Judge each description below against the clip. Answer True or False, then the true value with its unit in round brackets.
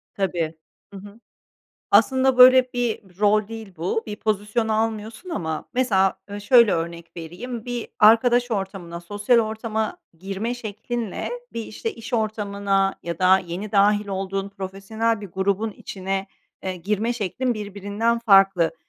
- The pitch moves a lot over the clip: False (2.8 semitones)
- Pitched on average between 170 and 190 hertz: False (205 Hz)